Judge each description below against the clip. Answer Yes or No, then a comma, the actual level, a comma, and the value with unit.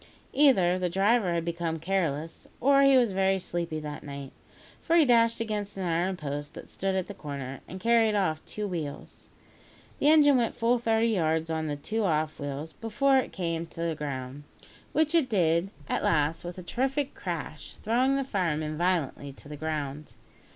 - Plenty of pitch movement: Yes, wide, 6.6 semitones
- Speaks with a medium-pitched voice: Yes, medium, 180 Hz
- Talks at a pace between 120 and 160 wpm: No, average, 185 wpm